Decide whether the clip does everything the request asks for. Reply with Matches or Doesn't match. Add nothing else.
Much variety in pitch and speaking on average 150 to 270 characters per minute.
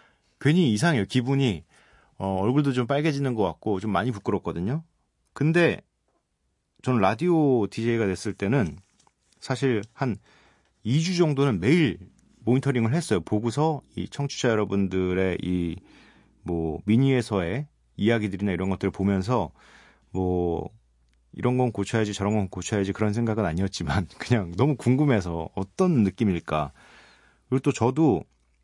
Doesn't match